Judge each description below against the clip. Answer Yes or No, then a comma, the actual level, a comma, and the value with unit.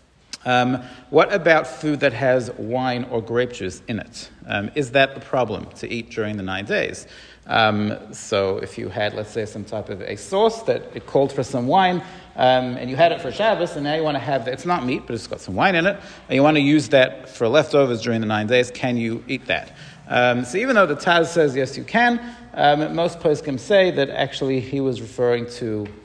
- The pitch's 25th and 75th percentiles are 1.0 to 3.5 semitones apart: No, average, 4.5 semitones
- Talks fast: Yes, fast, 230 wpm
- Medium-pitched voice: No, low, 130 Hz